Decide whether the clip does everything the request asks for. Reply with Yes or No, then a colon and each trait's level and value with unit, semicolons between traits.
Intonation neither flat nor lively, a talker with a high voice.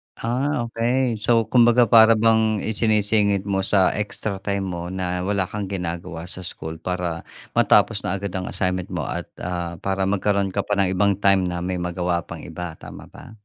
No: average, 3.0 semitones; low, 100 Hz